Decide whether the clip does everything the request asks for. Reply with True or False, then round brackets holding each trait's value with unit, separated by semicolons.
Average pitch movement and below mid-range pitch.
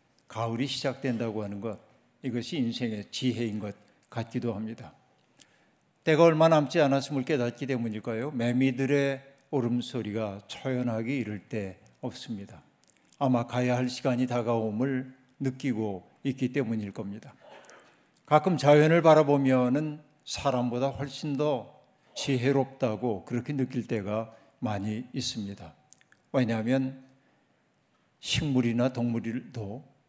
True (3.2 semitones; 125 Hz)